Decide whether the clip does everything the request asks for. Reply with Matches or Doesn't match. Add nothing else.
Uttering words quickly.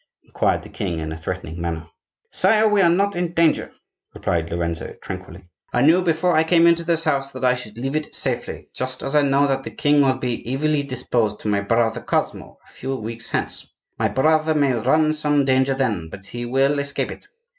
Matches